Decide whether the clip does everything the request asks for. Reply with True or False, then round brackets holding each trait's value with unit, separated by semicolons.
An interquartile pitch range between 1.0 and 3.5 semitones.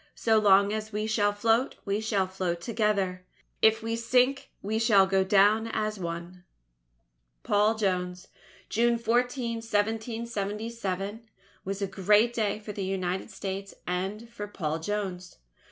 True (2.7 semitones)